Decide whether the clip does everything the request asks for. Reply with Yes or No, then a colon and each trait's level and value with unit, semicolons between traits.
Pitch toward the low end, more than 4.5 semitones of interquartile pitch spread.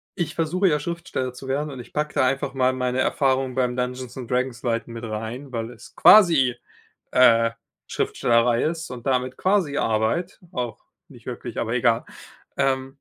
No: low, 130 Hz; average, 2.8 semitones